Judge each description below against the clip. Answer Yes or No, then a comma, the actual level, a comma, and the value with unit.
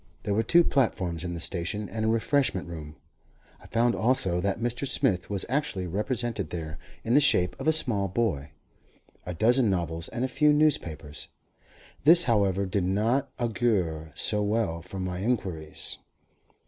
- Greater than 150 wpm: Yes, average, 160 wpm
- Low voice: Yes, low, 100 Hz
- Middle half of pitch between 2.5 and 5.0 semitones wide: No, wide, 5.4 semitones